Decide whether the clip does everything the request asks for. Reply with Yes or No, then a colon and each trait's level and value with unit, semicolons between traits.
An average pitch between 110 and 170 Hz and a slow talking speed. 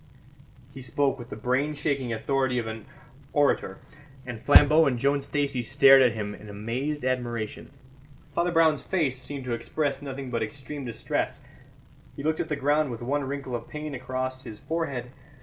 No: low, 135 Hz; average, 170 wpm